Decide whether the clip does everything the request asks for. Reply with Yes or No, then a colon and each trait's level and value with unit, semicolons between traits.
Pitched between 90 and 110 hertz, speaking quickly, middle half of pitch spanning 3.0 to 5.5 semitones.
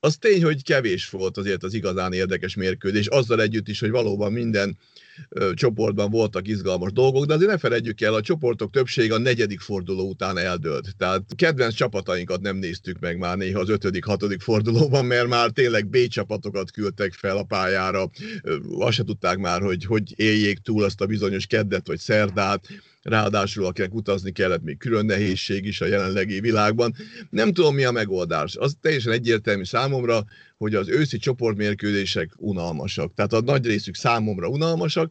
Yes: low, 105 Hz; fast, 170 wpm; average, 3.4 semitones